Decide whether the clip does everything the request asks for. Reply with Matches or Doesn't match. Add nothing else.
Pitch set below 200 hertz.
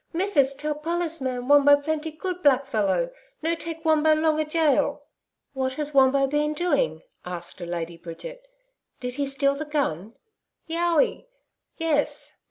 Doesn't match